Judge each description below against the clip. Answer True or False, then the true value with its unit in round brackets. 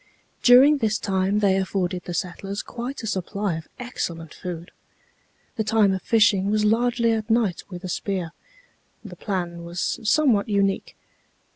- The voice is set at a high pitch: True (200 Hz)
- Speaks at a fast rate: False (150 wpm)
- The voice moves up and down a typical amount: True (3.5 semitones)